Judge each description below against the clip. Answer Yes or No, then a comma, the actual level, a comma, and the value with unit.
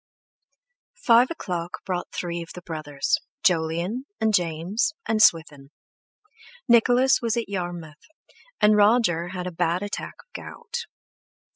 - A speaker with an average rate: No, slow, 125 wpm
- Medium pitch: Yes, medium, 180 Hz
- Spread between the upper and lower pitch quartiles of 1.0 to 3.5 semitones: No, wide, 5.4 semitones